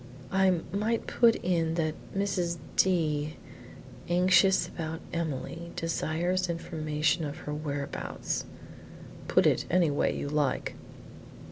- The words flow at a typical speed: No, slow, 115 wpm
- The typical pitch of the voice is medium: Yes, medium, 165 Hz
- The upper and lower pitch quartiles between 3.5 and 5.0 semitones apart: No, average, 3.1 semitones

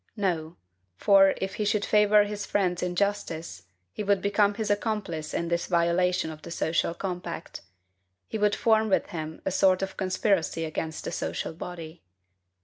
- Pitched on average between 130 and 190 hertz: Yes, medium, 185 Hz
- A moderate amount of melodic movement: Yes, average, 3.4 semitones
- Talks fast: No, average, 160 wpm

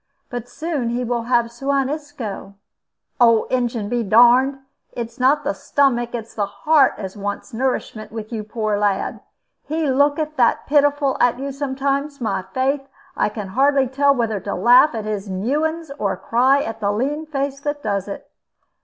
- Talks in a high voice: Yes, high, 245 Hz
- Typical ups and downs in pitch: Yes, average, 4.2 semitones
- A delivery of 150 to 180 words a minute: Yes, average, 170 wpm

